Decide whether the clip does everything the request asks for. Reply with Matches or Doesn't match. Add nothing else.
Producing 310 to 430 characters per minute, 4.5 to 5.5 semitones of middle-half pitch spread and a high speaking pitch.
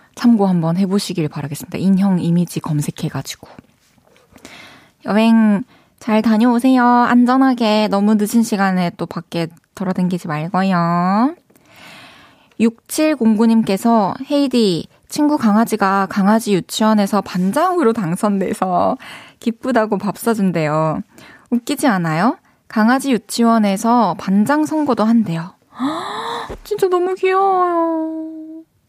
Doesn't match